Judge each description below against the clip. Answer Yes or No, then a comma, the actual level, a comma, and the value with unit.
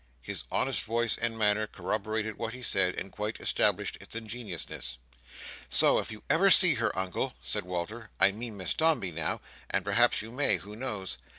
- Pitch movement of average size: Yes, average, 3.6 semitones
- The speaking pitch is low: Yes, low, 110 Hz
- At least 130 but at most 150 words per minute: No, average, 175 wpm